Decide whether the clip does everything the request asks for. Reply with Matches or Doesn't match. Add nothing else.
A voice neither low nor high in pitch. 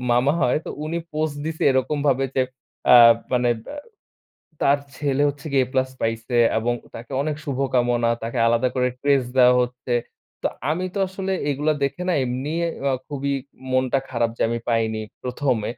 Doesn't match